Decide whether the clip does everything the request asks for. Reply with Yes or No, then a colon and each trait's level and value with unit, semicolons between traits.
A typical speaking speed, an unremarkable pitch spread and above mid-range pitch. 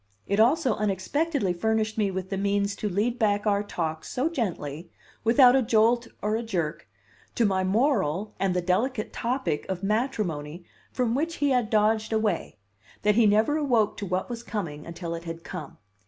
Yes: average, 180 wpm; average, 4.3 semitones; high, 210 Hz